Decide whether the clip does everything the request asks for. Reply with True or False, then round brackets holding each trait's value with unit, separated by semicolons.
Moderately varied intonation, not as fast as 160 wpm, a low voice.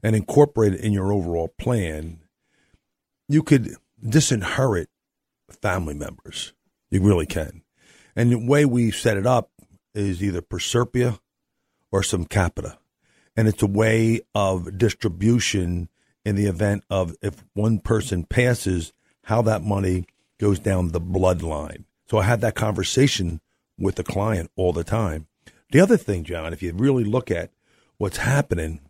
True (4.0 semitones; 145 wpm; 100 Hz)